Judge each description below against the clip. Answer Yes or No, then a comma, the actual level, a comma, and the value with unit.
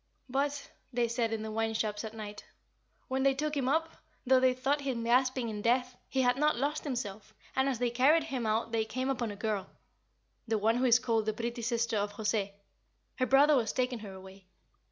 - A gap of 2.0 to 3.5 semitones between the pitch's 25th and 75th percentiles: Yes, average, 3.2 semitones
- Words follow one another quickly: Yes, fast, 215 wpm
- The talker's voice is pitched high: Yes, high, 240 Hz